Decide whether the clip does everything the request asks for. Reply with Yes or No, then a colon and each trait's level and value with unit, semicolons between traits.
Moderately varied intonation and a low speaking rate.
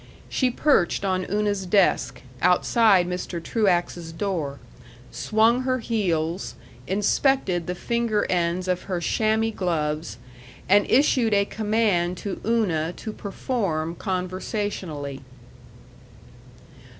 Yes: average, 4.0 semitones; slow, 100 wpm